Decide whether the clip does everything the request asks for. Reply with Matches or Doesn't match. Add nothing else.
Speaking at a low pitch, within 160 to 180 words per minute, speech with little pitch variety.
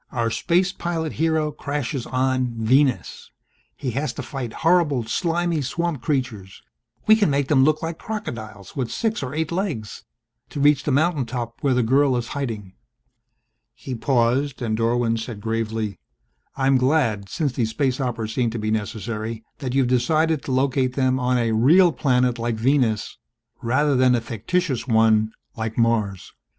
Doesn't match